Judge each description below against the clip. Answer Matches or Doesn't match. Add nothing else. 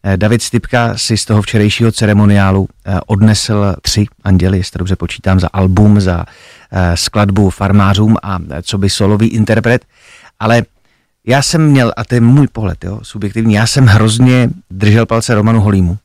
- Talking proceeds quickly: Doesn't match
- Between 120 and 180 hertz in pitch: Doesn't match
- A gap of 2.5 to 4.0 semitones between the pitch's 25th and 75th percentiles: Matches